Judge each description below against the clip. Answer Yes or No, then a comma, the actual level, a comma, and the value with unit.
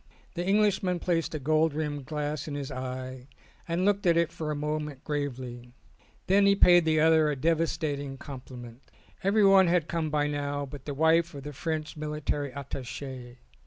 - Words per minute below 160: No, average, 175 wpm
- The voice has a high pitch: No, medium, 150 Hz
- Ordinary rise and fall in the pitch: Yes, average, 3.3 semitones